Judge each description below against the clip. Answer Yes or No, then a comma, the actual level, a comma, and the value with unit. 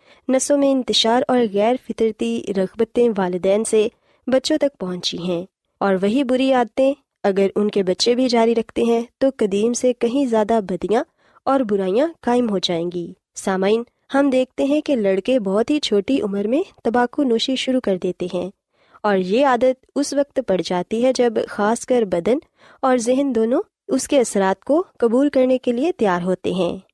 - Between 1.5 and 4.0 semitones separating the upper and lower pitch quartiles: No, average, 4.6 semitones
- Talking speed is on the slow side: No, average, 180 wpm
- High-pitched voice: Yes, high, 235 Hz